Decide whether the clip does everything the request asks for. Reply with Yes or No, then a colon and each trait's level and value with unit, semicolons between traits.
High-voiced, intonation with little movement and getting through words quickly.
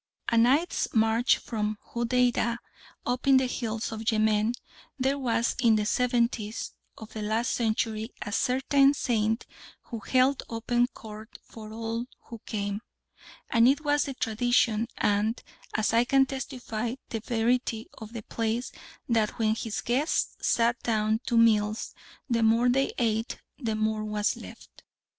No: high, 230 Hz; narrow, 2.2 semitones; average, 150 wpm